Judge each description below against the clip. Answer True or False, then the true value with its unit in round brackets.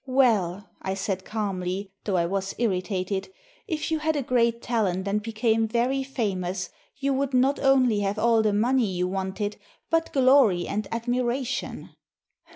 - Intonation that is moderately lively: True (4.7 semitones)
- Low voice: False (220 Hz)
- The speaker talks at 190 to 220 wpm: False (155 wpm)